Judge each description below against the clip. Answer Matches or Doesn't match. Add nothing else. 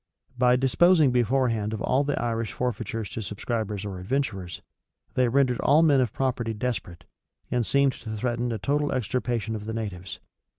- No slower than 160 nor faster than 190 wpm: Matches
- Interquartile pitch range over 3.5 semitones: Doesn't match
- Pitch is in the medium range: Doesn't match